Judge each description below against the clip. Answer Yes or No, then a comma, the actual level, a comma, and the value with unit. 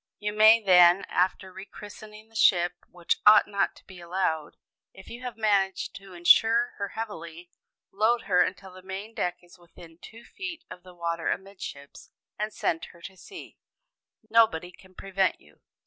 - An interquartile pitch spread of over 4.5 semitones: No, average, 3.4 semitones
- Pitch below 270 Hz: Yes, high, 190 Hz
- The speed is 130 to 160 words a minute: No, average, 170 wpm